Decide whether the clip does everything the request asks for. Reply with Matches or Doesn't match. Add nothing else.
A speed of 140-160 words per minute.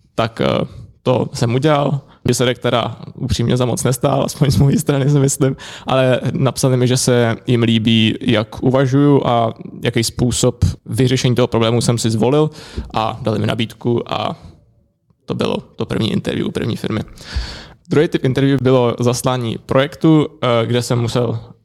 Matches